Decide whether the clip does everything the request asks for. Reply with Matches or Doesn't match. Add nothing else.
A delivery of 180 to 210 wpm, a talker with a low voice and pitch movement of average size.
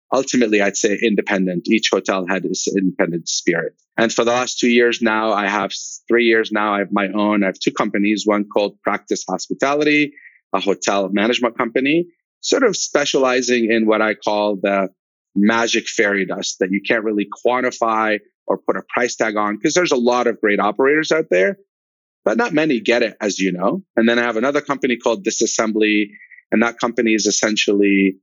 Matches